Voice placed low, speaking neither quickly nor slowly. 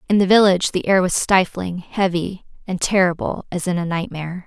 No: medium, 185 Hz; average, 190 wpm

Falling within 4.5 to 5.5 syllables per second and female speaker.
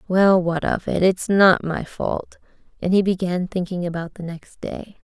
No: 4.3 syllables/s; female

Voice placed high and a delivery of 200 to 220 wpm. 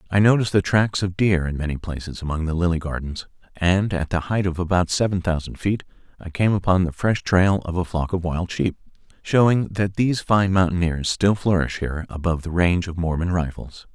No: very low, 90 Hz; fast, 205 wpm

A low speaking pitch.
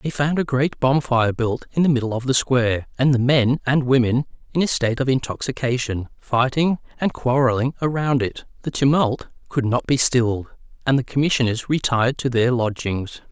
Yes: low, 130 Hz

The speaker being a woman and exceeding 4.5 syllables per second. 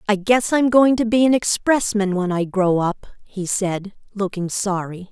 No: female; 4.3 syllables/s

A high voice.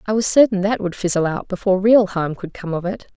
Yes: high, 195 Hz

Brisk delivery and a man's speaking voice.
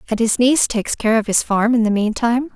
No: fast, 260 wpm; female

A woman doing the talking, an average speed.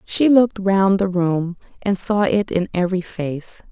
Yes: female; average, 180 wpm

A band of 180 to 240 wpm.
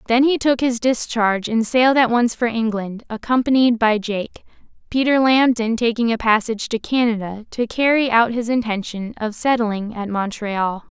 No: average, 165 wpm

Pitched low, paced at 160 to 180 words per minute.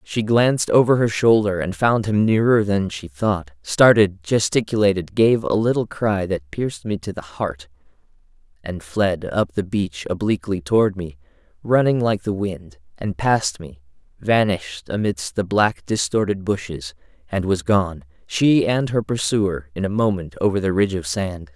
Yes: very low, 95 Hz; average, 165 wpm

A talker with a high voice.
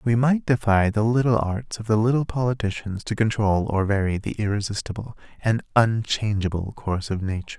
No: low, 110 Hz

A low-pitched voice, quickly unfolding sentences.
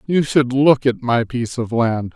Yes: low, 125 Hz; fast, 220 wpm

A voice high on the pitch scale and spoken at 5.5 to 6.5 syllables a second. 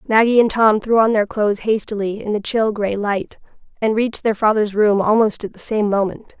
No: high, 210 Hz; 5.3 syllables/s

